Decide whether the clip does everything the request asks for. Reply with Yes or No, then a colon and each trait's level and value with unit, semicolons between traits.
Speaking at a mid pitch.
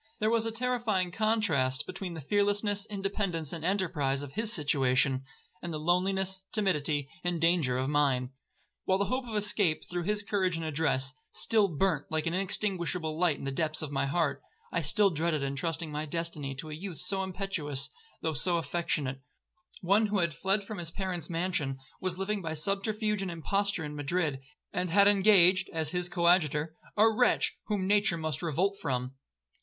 Yes: medium, 175 Hz